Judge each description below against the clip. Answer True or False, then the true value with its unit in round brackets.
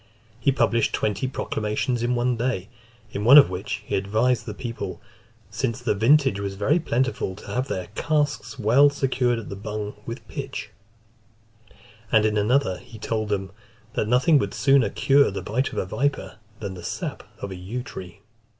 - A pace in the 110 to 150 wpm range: False (175 wpm)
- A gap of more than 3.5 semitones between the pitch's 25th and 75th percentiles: True (4.3 semitones)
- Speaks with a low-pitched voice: True (115 Hz)